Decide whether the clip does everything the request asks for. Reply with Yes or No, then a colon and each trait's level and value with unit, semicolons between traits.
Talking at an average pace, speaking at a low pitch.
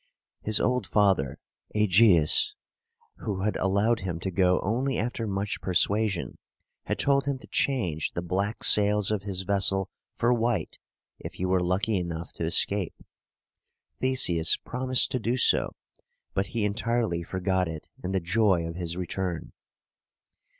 Yes: average, 145 wpm; low, 100 Hz